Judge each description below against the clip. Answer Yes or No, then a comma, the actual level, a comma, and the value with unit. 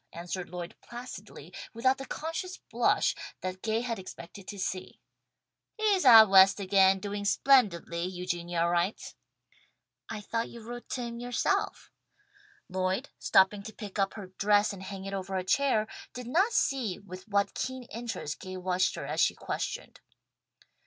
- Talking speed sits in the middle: Yes, average, 160 wpm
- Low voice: No, high, 200 Hz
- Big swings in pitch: No, average, 4.2 semitones